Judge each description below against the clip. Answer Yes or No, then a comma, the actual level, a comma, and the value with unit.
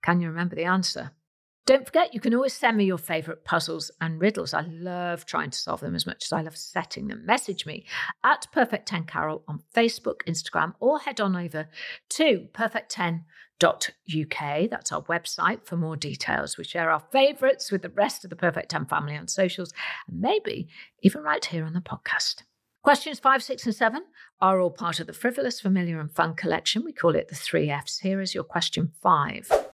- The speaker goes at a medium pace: Yes, average, 195 wpm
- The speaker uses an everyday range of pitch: No, wide, 6.0 semitones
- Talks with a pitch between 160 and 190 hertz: Yes, medium, 185 Hz